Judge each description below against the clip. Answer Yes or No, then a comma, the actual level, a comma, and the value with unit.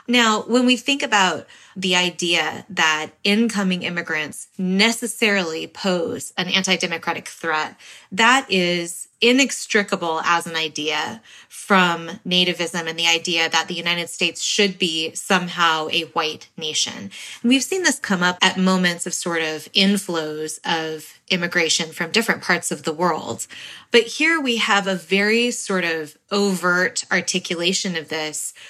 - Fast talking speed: No, average, 140 wpm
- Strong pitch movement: No, average, 3.4 semitones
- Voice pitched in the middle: Yes, medium, 180 Hz